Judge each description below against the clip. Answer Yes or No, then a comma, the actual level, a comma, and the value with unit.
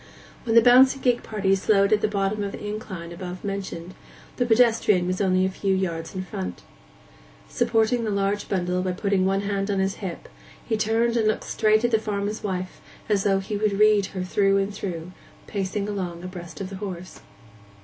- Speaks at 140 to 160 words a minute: No, average, 195 wpm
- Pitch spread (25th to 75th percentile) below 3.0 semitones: Yes, narrow, 2.4 semitones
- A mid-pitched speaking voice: No, high, 200 Hz